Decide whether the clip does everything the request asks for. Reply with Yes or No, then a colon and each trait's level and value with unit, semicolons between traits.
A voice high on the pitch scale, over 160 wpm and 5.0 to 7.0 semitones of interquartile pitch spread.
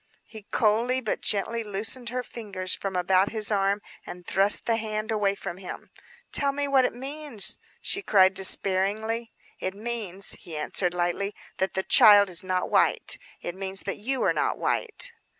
No: high, 205 Hz; average, 170 wpm; average, 3.4 semitones